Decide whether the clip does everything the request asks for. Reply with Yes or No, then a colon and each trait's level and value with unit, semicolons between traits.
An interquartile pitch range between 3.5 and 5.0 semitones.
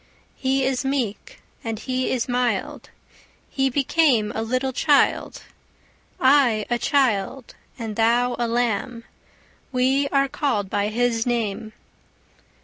No: average, 3.0 semitones